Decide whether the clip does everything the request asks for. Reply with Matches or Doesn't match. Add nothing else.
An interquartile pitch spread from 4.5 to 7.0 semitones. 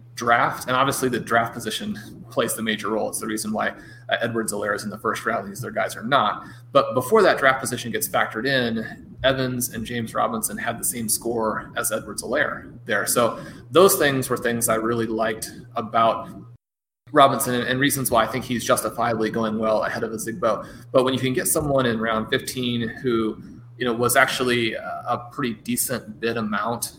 Doesn't match